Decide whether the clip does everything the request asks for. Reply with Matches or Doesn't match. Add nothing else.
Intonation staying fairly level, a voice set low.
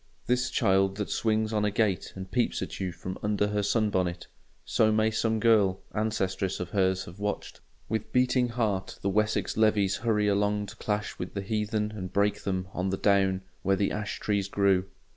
Matches